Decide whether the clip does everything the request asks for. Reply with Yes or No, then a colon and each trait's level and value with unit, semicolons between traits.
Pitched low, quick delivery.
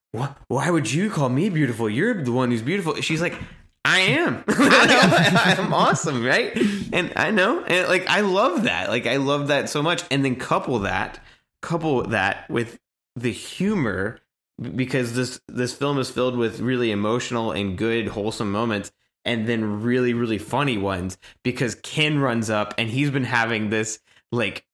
No: low, 125 Hz; average, 175 wpm